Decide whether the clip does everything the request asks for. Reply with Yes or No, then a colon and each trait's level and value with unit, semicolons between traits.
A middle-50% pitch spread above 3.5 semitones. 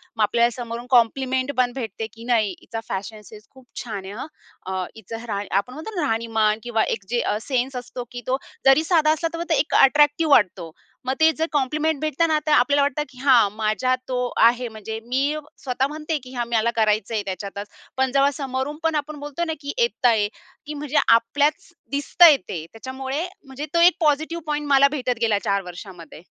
Yes: average, 4.7 semitones